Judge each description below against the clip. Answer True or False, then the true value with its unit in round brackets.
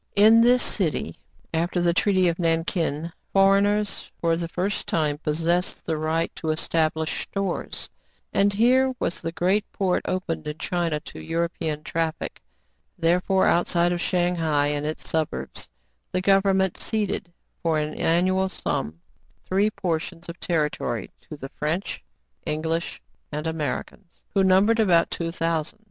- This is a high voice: False (170 Hz)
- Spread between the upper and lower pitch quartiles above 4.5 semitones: False (3.1 semitones)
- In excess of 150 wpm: False (145 wpm)